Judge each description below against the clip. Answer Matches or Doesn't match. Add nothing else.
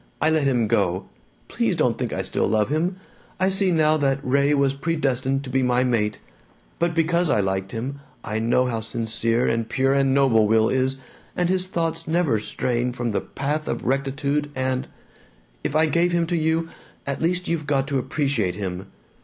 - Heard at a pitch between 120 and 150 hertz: Matches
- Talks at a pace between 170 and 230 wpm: Matches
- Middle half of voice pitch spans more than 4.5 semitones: Matches